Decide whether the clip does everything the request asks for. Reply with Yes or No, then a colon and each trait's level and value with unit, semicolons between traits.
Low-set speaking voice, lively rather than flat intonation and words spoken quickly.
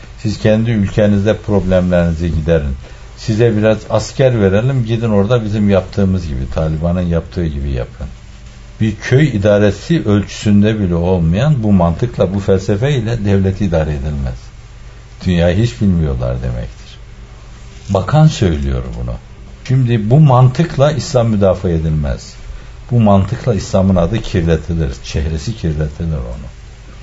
No: low, 100 Hz; wide, 5.9 semitones; average, 120 wpm